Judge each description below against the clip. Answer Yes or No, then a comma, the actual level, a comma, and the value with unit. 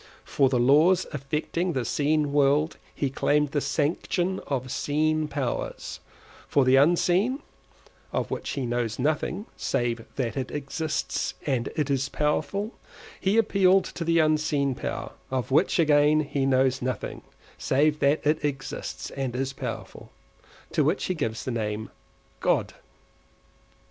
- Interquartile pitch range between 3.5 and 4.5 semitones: No, average, 2.9 semitones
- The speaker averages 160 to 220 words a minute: No, average, 140 wpm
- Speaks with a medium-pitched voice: Yes, medium, 145 Hz